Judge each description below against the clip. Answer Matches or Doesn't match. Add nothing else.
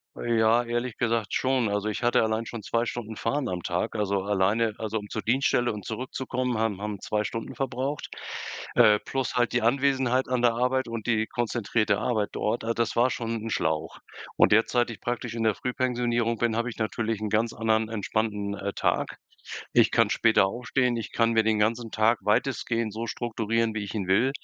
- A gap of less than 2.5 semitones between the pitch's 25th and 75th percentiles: Matches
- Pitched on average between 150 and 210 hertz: Doesn't match